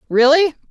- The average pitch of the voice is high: Yes, very high, 295 Hz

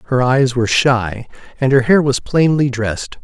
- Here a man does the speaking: Yes, male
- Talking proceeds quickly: No, average, 185 wpm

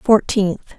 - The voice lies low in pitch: No, high, 205 Hz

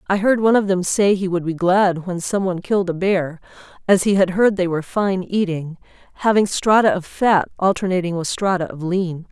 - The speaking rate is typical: No, fast, 210 wpm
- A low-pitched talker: No, medium, 185 Hz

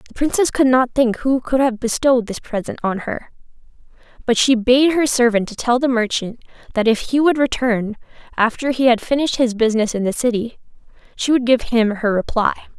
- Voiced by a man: No, female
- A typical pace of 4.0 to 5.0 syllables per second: No, 5.6 syllables/s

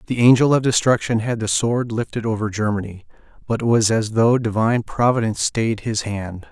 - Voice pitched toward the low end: Yes, low, 110 Hz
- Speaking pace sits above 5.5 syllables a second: No, 5.4 syllables/s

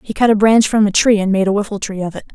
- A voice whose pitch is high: Yes, high, 205 Hz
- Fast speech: Yes, fast, 360 wpm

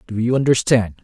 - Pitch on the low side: Yes, low, 120 Hz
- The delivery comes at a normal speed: Yes, average, 175 wpm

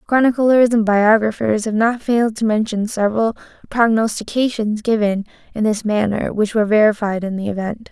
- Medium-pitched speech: No, high, 220 Hz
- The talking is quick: No, average, 150 wpm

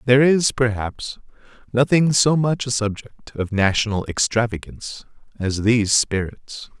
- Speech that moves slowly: Yes, slow, 125 wpm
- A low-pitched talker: Yes, low, 115 Hz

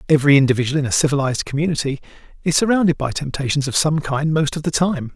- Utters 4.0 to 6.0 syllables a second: No, 7.0 syllables/s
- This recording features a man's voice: Yes, male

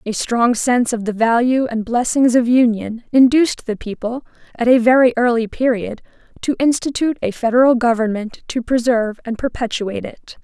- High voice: Yes, high, 240 Hz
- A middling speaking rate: Yes, average, 160 wpm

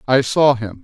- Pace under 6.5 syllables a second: Yes, 4.5 syllables/s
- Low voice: Yes, low, 125 Hz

